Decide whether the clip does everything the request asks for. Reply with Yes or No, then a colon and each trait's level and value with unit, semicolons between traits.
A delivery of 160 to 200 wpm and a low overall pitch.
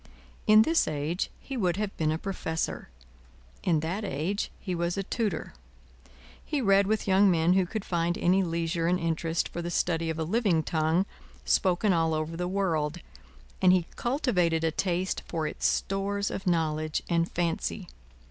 No: average, 170 wpm; medium, 175 Hz